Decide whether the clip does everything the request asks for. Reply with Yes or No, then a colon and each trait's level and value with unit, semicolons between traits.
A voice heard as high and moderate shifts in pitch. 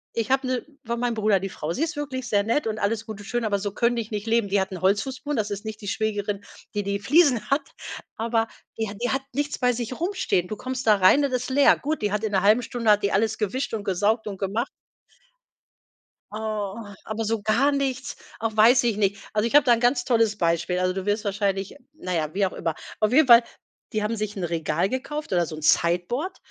Yes: high, 220 Hz; average, 3.5 semitones